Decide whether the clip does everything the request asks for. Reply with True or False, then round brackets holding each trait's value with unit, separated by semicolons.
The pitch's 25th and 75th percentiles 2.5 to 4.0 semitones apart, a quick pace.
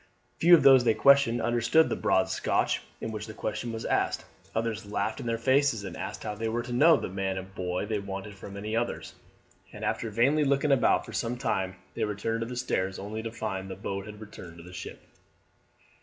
True (3.5 semitones; 225 wpm)